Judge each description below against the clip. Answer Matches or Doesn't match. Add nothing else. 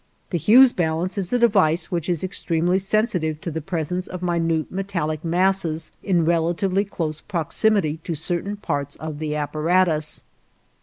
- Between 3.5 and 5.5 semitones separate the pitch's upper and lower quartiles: Doesn't match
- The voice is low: Doesn't match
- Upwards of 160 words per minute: Doesn't match